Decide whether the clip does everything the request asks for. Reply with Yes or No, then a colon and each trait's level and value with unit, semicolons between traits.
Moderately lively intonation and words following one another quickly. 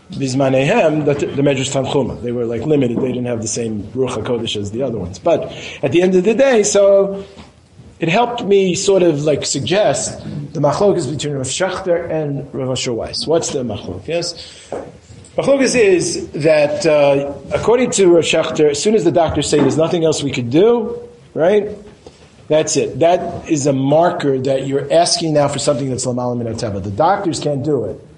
No: average, 5.0 semitones; average, 185 wpm